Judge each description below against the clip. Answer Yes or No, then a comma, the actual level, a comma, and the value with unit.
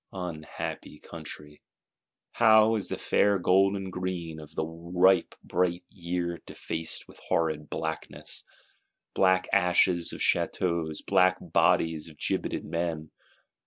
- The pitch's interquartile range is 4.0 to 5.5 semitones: No, narrow, 2.5 semitones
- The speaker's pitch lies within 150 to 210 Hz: No, very low, 85 Hz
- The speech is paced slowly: Yes, slow, 120 wpm